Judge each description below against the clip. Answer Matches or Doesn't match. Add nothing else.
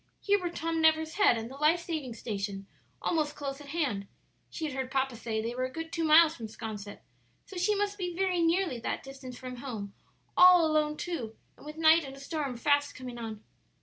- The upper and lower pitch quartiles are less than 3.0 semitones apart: Doesn't match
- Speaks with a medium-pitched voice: Doesn't match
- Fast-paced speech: Matches